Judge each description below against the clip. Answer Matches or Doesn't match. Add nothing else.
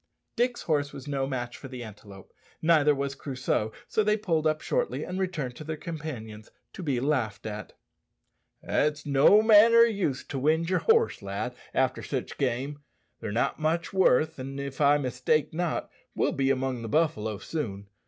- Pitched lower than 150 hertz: Matches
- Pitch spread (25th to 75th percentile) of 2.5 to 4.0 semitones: Doesn't match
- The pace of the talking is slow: Doesn't match